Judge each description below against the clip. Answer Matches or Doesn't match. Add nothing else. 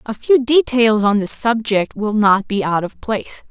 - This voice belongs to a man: Doesn't match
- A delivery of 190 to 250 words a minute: Matches